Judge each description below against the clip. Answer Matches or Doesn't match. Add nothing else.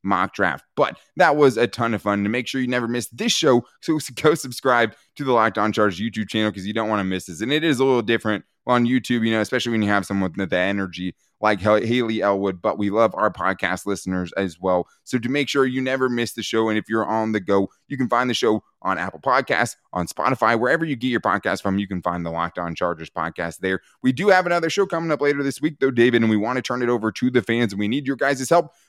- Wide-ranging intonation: Doesn't match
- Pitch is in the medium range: Doesn't match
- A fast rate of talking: Matches